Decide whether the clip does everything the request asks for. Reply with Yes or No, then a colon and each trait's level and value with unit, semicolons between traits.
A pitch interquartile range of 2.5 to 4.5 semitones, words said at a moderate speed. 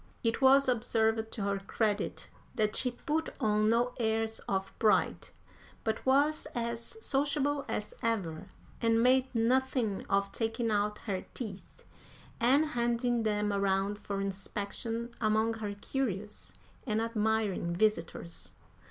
No: average, 2.8 semitones; slow, 125 wpm